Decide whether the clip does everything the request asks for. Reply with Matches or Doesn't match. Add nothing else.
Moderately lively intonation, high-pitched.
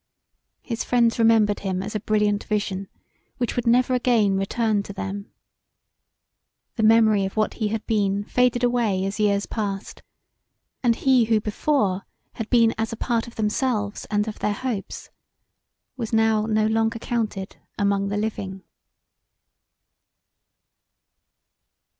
Doesn't match